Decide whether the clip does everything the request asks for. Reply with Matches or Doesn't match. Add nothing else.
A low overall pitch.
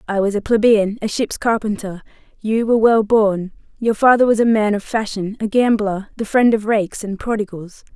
Doesn't match